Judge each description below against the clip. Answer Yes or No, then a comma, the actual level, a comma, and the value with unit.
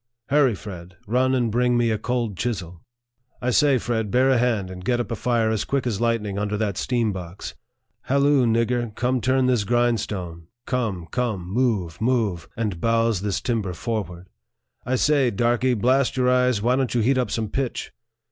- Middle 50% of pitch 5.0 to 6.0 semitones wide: No, average, 3.5 semitones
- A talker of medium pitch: No, low, 115 Hz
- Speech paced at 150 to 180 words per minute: No, average, 200 wpm